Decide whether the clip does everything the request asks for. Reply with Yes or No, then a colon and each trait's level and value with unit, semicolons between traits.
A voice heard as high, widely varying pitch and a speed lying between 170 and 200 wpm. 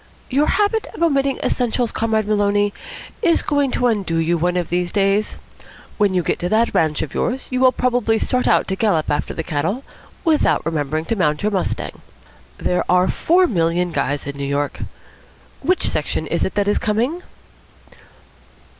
Yes: high, 205 Hz; wide, 7.0 semitones; average, 175 wpm